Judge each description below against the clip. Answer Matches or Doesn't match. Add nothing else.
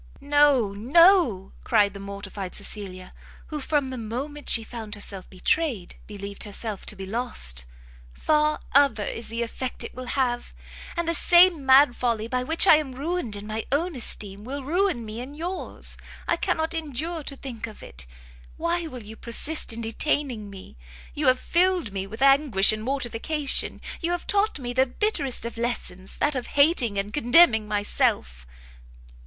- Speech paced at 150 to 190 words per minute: Matches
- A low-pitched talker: Doesn't match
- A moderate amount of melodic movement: Doesn't match